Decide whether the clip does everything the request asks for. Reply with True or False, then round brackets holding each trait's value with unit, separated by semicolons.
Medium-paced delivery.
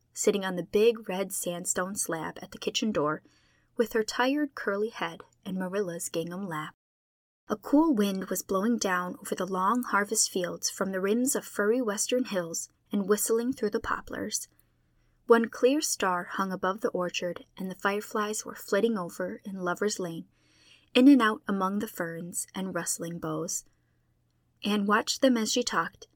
True (170 wpm)